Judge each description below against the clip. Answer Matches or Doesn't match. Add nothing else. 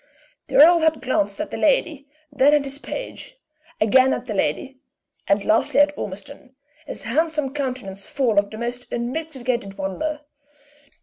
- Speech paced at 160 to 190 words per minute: Doesn't match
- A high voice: Matches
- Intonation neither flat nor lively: Matches